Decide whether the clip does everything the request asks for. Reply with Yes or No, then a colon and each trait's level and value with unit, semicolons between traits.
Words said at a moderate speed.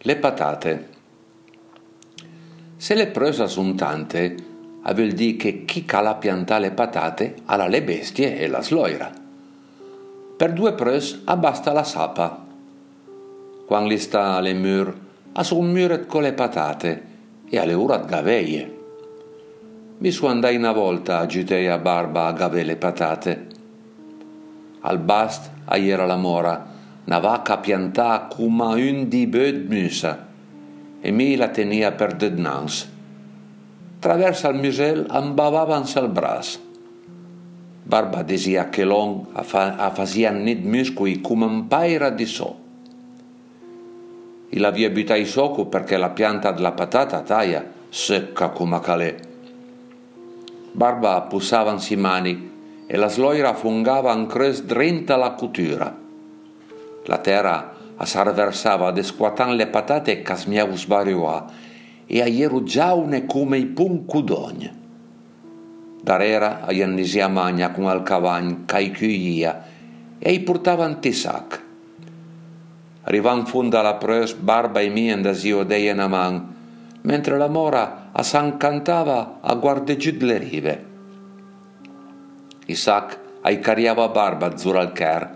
Yes: average, 125 wpm